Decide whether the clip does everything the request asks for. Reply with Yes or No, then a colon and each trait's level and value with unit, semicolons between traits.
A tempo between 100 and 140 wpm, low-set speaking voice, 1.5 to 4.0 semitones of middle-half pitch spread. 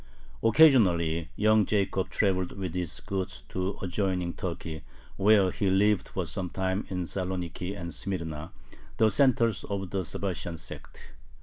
Yes: slow, 135 wpm; very low, 95 Hz; narrow, 2.4 semitones